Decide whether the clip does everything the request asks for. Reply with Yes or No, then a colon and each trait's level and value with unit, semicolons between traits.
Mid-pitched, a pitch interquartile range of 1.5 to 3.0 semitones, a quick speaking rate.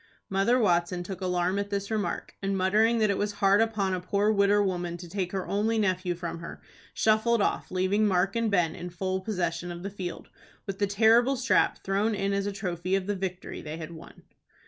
No: high, 195 Hz; narrow, 2.4 semitones; fast, 215 wpm